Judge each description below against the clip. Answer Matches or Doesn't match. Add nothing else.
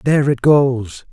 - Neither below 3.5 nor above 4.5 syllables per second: Matches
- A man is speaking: Matches